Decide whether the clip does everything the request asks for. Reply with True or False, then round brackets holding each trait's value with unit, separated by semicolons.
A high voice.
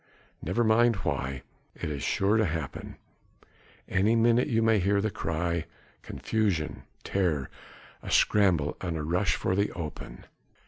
False (95 Hz)